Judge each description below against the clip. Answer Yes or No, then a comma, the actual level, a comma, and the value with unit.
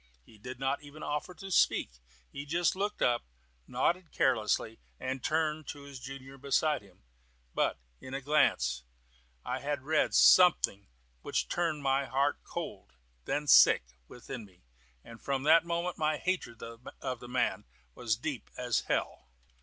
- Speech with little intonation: No, average, 4.0 semitones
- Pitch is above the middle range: No, low, 135 Hz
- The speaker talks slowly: No, average, 155 wpm